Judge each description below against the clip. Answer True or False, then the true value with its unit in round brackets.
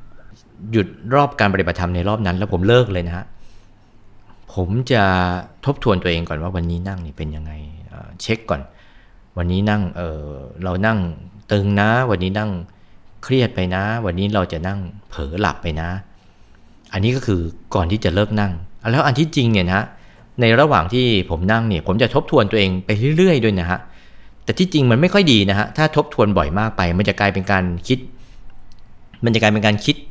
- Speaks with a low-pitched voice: True (100 Hz)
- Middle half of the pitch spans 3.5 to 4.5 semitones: True (3.9 semitones)